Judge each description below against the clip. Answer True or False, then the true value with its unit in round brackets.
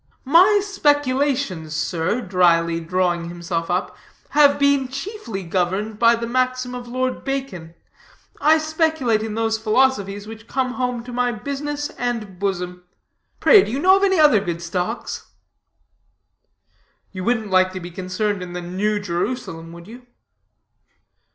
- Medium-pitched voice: False (220 Hz)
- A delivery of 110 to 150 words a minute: True (145 wpm)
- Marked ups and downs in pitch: True (6.5 semitones)